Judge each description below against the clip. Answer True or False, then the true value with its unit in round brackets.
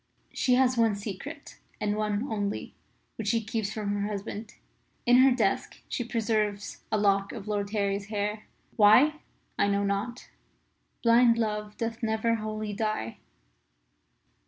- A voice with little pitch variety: True (2.1 semitones)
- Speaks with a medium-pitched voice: False (215 Hz)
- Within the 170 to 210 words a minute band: False (140 wpm)